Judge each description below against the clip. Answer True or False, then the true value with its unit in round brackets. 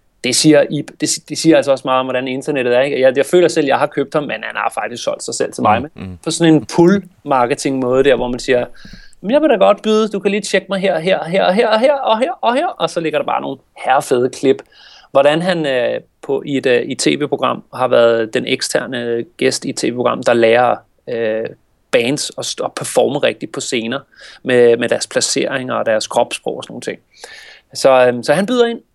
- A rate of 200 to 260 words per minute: True (225 wpm)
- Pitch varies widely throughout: True (7.6 semitones)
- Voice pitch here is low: False (150 Hz)